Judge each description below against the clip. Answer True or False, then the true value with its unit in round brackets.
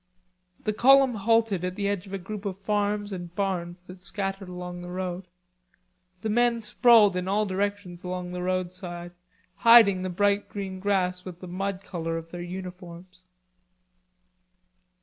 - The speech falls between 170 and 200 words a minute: False (155 wpm)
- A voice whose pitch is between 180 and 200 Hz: True (190 Hz)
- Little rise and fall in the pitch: True (2.3 semitones)